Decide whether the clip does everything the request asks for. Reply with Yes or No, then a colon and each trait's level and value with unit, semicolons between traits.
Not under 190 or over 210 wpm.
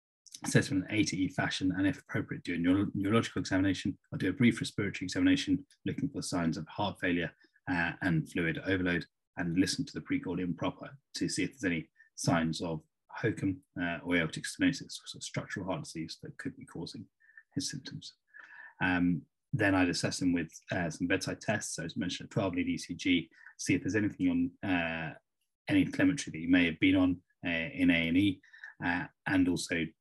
Yes: average, 200 wpm